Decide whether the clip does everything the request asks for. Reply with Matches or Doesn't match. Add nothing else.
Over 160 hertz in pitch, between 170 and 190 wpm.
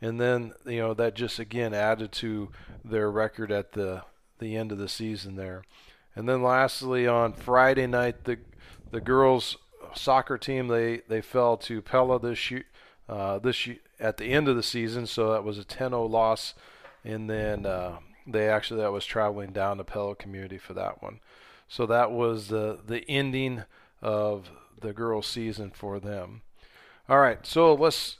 Doesn't match